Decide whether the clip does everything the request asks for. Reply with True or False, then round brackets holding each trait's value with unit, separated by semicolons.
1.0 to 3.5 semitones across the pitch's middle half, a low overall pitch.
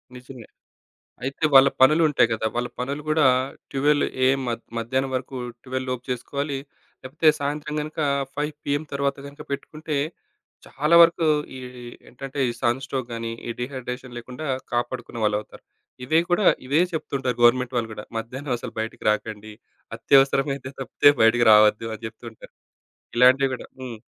True (2.9 semitones; 130 Hz)